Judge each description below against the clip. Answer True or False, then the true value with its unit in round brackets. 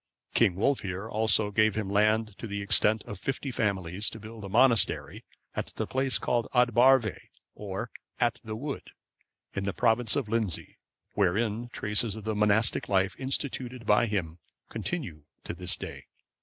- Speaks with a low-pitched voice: True (110 Hz)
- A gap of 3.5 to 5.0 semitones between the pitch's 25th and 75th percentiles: False (3.0 semitones)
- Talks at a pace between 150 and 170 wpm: True (160 wpm)